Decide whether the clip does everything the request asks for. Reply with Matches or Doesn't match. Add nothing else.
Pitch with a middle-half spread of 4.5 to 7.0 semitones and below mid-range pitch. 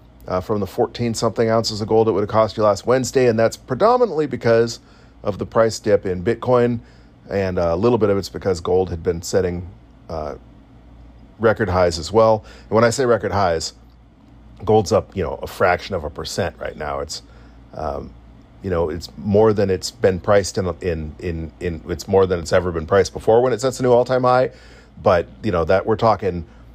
Matches